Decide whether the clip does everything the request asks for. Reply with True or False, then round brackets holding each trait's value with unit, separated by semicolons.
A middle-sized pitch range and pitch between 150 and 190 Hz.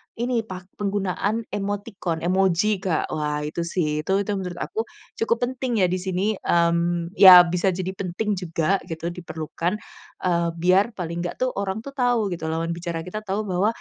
True (3.4 semitones; 185 Hz)